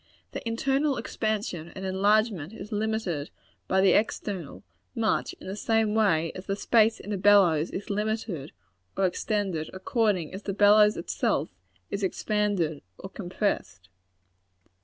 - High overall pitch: Yes, high, 200 Hz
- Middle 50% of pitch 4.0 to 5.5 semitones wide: No, average, 3.0 semitones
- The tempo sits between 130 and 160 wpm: Yes, average, 140 wpm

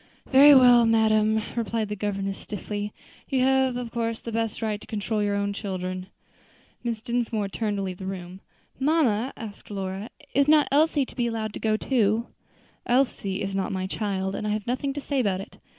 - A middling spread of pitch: Yes, average, 3.4 semitones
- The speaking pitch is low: No, high, 215 Hz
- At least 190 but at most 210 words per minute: Yes, average, 195 wpm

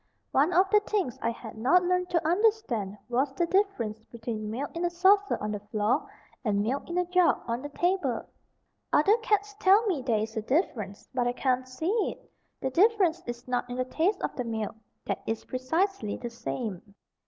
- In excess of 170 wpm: Yes, average, 200 wpm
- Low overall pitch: No, very high, 265 Hz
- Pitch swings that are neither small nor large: No, wide, 7.8 semitones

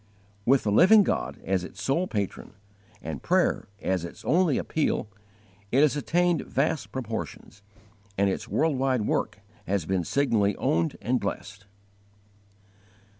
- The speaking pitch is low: Yes, low, 110 Hz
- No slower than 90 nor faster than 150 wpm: Yes, slow, 135 wpm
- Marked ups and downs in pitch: Yes, wide, 6.9 semitones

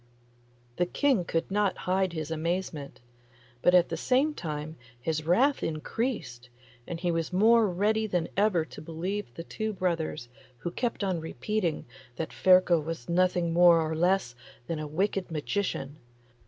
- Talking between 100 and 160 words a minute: Yes, average, 155 wpm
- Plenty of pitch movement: No, average, 3.6 semitones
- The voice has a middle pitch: Yes, medium, 175 Hz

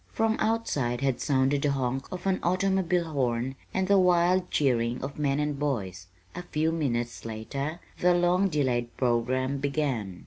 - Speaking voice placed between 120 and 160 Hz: Yes, medium, 140 Hz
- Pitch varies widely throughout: Yes, wide, 6.1 semitones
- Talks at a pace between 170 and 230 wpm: No, average, 160 wpm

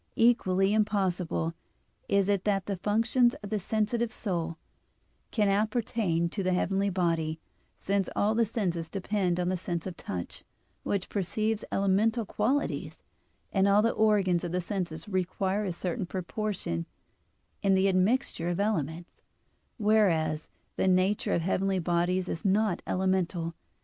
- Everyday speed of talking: Yes, average, 145 wpm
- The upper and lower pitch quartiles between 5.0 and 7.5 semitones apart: No, average, 3.1 semitones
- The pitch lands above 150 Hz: Yes, high, 190 Hz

